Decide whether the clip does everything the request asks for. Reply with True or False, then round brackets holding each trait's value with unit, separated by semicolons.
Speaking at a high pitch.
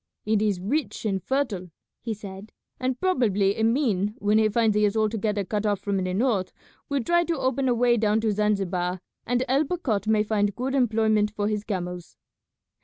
True (215 Hz)